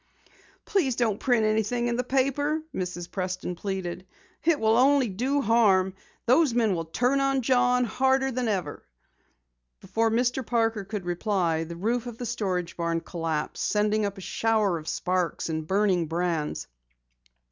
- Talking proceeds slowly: No, average, 155 wpm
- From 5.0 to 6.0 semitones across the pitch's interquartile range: Yes, wide, 5.4 semitones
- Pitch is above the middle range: Yes, high, 215 Hz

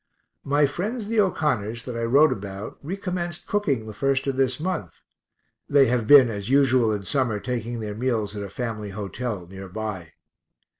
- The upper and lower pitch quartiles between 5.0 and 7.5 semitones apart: Yes, average, 5.3 semitones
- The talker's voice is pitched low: Yes, low, 120 Hz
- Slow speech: No, average, 170 wpm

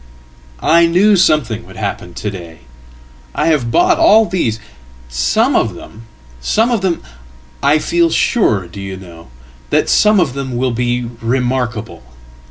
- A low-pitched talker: Yes, low, 125 Hz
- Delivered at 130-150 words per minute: Yes, average, 145 wpm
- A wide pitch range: Yes, wide, 9.0 semitones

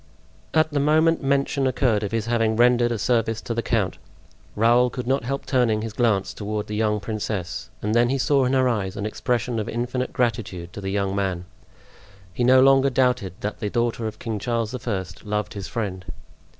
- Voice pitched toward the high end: No, low, 115 Hz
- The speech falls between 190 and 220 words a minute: Yes, average, 200 wpm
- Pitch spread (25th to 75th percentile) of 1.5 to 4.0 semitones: Yes, average, 3.1 semitones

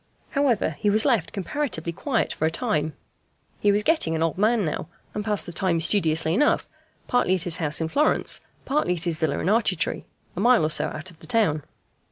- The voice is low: No, medium, 185 Hz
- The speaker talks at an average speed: No, fast, 210 wpm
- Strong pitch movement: Yes, wide, 5.8 semitones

